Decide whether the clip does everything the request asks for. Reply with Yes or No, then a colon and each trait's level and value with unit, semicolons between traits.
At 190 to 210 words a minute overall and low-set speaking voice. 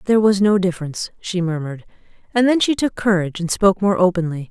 No: average, 200 wpm; high, 190 Hz